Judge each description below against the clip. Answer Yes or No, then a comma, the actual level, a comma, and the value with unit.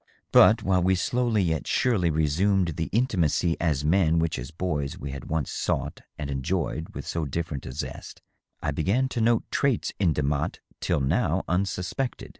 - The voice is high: No, very low, 85 Hz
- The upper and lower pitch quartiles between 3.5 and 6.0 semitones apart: Yes, average, 4.5 semitones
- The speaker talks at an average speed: Yes, average, 170 wpm